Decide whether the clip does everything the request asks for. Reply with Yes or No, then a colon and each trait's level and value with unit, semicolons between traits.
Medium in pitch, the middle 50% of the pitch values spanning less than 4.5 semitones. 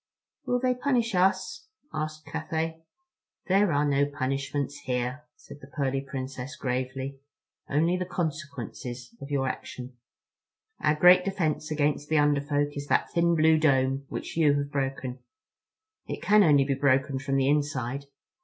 Yes: medium, 145 Hz; average, 2.9 semitones